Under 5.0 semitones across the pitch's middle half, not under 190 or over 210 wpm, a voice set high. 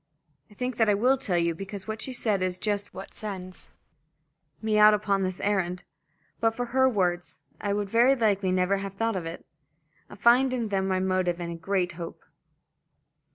Yes: average, 3.2 semitones; average, 195 wpm; high, 200 Hz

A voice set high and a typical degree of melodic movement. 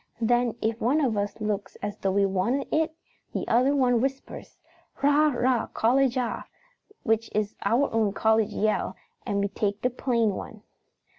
Yes: high, 230 Hz; average, 3.6 semitones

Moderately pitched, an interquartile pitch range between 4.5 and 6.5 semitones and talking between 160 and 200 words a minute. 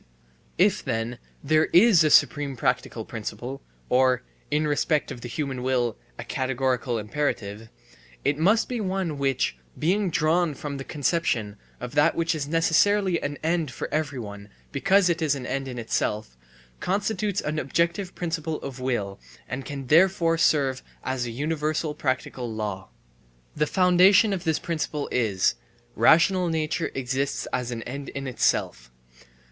No: medium, 145 Hz; average, 5.0 semitones; average, 150 wpm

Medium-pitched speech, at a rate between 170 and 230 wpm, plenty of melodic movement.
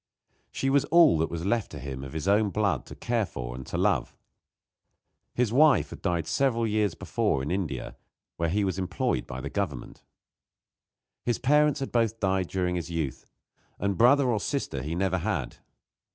No: very low, 95 Hz; average, 180 wpm; wide, 6.3 semitones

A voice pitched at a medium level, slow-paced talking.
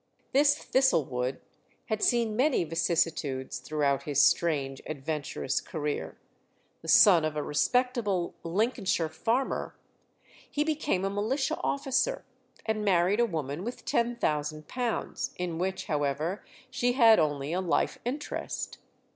Yes: medium, 180 Hz; slow, 120 wpm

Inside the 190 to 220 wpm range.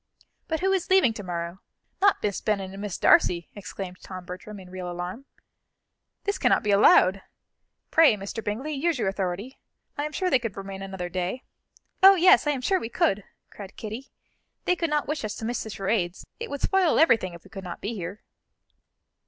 Yes: average, 200 wpm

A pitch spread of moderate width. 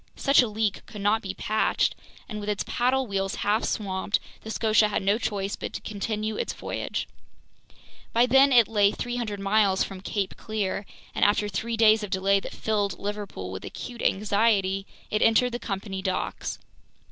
No: narrow, 2.1 semitones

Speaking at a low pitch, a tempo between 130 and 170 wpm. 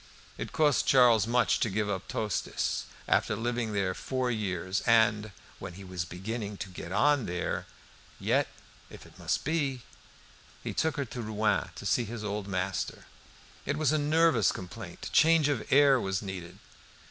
Yes: low, 110 Hz; average, 165 wpm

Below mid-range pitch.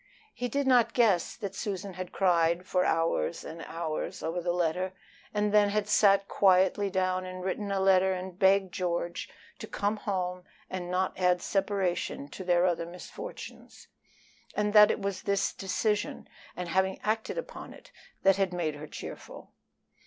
No: medium, 185 Hz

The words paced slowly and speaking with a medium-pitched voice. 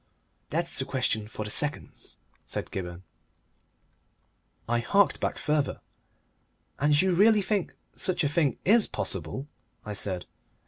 Yes: slow, 130 wpm; medium, 145 Hz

